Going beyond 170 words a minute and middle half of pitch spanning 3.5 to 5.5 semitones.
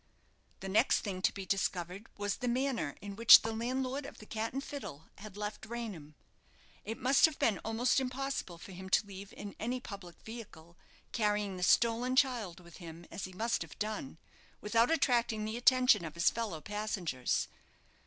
Yes: average, 180 wpm; average, 4.3 semitones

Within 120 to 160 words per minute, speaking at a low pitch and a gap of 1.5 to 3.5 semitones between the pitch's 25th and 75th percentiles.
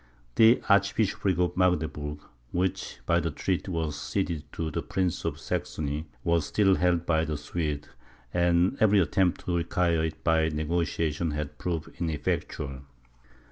Yes: average, 140 wpm; very low, 85 Hz; average, 2.8 semitones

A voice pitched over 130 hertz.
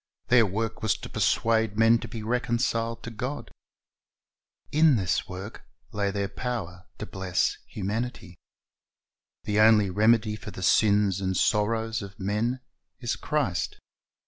No: low, 110 Hz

